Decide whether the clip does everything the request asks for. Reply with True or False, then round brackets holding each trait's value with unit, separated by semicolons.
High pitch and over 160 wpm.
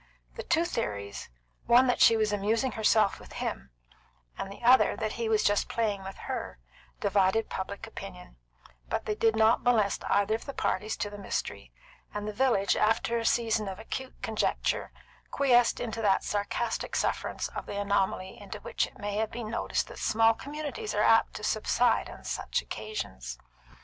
True (215 Hz; 175 wpm)